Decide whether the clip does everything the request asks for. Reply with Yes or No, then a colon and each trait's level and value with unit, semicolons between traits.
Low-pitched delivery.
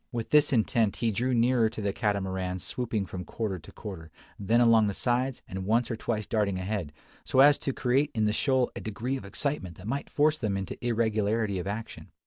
Yes: low, 110 Hz